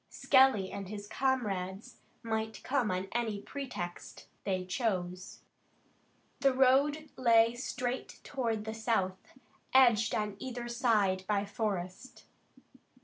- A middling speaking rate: No, slow, 110 wpm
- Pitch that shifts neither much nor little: Yes, average, 4.5 semitones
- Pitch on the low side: No, high, 220 Hz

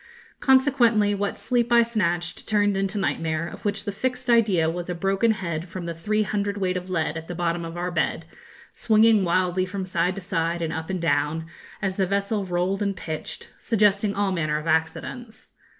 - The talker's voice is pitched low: No, high, 190 Hz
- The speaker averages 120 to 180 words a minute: No, average, 190 wpm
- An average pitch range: Yes, average, 3.5 semitones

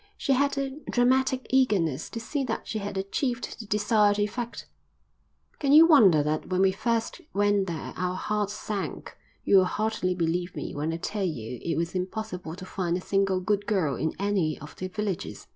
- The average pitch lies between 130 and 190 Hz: No, high, 200 Hz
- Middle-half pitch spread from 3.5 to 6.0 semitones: Yes, average, 3.8 semitones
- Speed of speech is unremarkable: Yes, average, 185 wpm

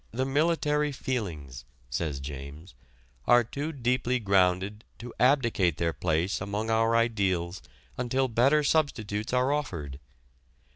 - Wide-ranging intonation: Yes, wide, 6.5 semitones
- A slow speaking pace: Yes, slow, 115 wpm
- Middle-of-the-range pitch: No, low, 115 Hz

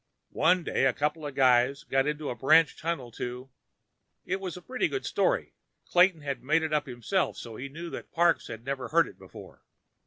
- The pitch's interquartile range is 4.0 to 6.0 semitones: Yes, average, 4.4 semitones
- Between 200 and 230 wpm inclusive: Yes, fast, 205 wpm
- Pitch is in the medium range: Yes, medium, 150 Hz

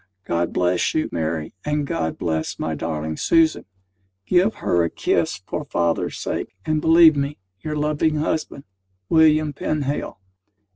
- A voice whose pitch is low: No, medium, 145 Hz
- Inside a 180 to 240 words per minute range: No, average, 140 wpm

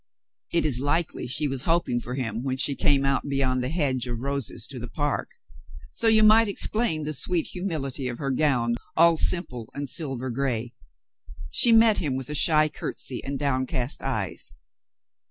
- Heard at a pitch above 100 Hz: Yes, medium, 140 Hz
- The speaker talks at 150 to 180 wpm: Yes, average, 175 wpm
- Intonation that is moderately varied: Yes, average, 3.8 semitones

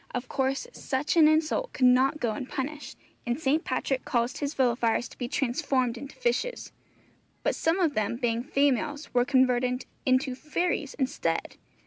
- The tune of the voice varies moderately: Yes, average, 3.4 semitones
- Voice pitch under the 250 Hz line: No, very high, 265 Hz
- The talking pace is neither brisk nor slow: Yes, average, 155 wpm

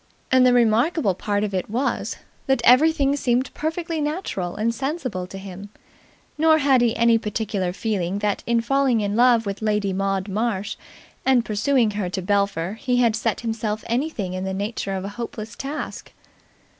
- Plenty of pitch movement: No, average, 4.2 semitones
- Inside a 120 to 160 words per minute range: No, average, 170 wpm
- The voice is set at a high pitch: Yes, high, 225 Hz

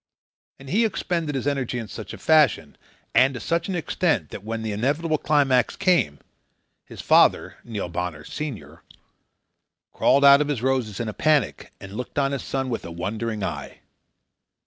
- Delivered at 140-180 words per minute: Yes, average, 170 wpm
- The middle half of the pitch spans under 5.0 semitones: No, wide, 5.5 semitones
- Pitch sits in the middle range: No, low, 130 Hz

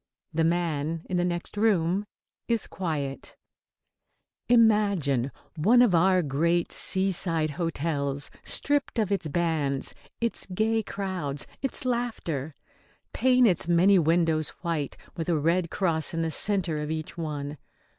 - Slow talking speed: Yes, slow, 130 wpm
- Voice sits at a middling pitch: Yes, medium, 170 Hz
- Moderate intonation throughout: Yes, average, 4.2 semitones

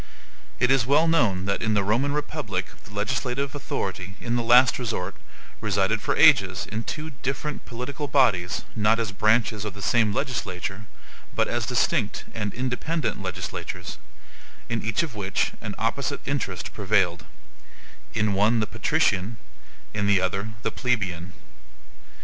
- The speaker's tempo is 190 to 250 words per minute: No, average, 145 wpm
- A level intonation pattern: No, average, 4.2 semitones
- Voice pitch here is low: Yes, low, 110 Hz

